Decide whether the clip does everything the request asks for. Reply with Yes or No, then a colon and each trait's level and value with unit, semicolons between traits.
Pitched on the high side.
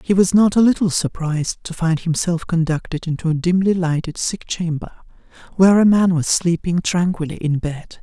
No: medium, 170 Hz